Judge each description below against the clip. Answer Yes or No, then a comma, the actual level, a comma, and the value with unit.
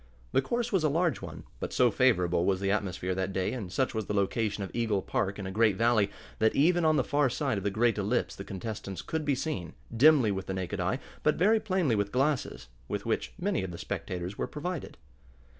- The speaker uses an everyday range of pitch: No, wide, 7.2 semitones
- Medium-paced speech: No, fast, 225 wpm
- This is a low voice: Yes, low, 110 Hz